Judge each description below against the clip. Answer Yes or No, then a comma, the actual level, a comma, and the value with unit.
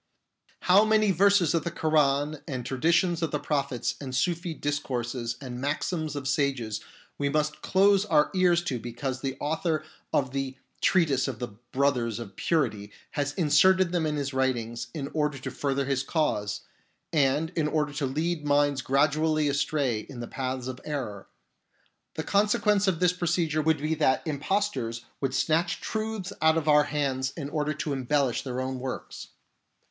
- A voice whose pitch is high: No, medium, 145 Hz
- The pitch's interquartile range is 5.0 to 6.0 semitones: No, average, 3.6 semitones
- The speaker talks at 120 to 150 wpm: No, average, 165 wpm